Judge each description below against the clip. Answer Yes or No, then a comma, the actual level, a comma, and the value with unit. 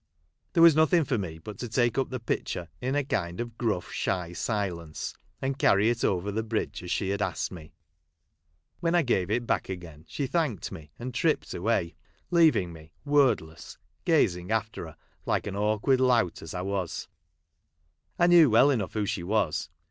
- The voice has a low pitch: Yes, low, 110 Hz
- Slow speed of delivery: No, average, 190 wpm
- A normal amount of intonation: No, wide, 6.5 semitones